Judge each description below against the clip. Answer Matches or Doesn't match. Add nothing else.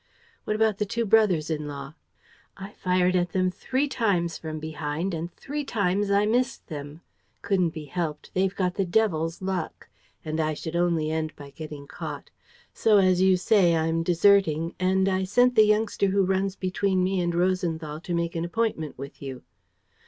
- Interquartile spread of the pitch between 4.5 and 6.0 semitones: Doesn't match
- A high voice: Doesn't match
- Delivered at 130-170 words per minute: Doesn't match